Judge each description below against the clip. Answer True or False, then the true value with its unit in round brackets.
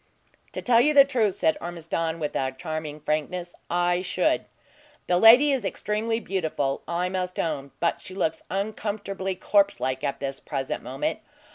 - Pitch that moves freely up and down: False (4.6 semitones)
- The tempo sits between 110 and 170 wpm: True (155 wpm)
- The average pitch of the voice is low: False (180 Hz)